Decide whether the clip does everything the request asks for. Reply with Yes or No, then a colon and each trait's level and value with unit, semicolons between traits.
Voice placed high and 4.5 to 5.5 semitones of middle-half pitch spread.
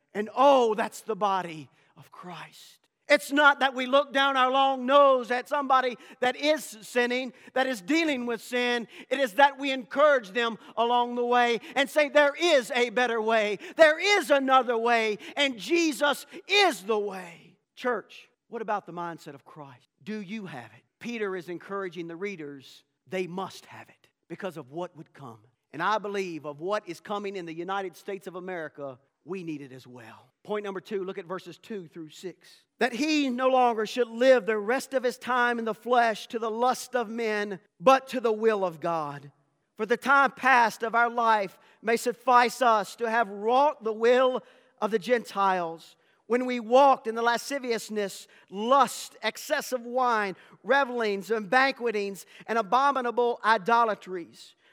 Yes: high, 230 Hz; average, 5.1 semitones